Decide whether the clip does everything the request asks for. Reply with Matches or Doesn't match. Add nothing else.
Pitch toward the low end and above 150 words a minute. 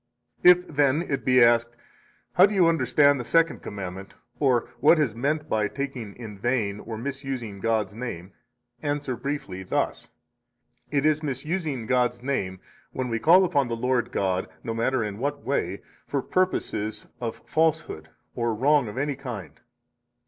Matches